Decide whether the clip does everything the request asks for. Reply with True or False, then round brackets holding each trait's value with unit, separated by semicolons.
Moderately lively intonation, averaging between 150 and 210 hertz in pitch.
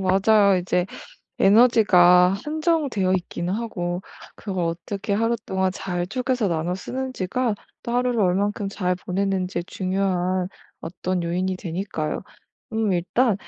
True (3.5 semitones; 190 Hz)